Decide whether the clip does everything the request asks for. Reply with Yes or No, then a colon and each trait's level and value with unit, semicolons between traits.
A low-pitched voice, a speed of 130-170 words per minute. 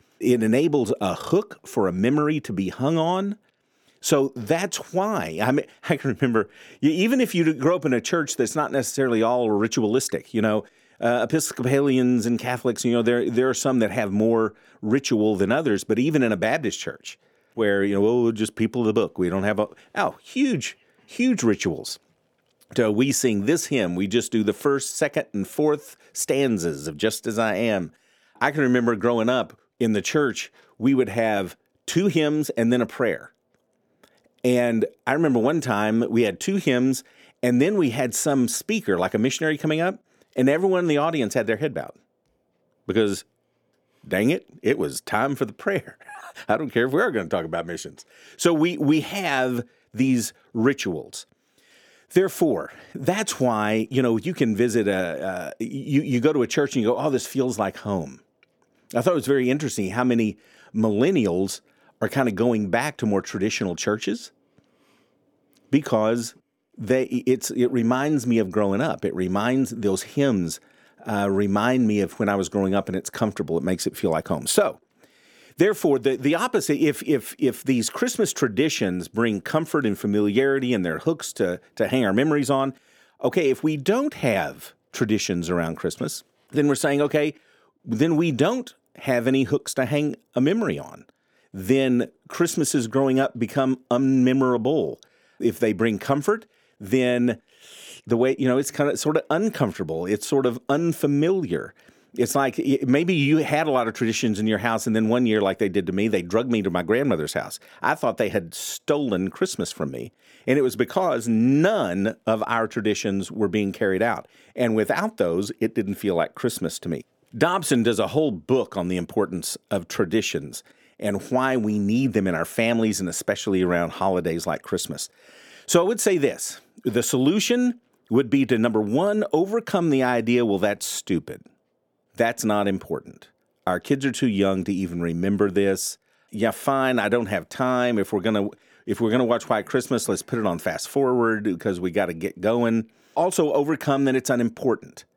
No: low, 125 Hz; average, 190 wpm